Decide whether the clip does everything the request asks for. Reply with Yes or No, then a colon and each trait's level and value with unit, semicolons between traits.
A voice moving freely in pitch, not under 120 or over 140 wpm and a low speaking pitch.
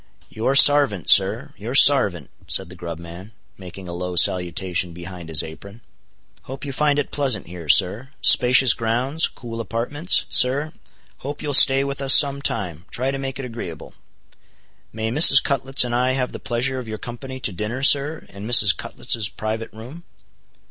No: wide, 6.4 semitones; average, 160 wpm; low, 120 Hz